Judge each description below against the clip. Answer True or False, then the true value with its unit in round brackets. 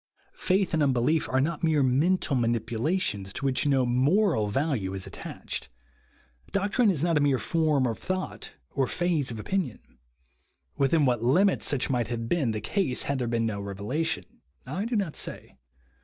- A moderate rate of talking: True (170 wpm)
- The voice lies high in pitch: False (140 Hz)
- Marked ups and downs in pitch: True (6.0 semitones)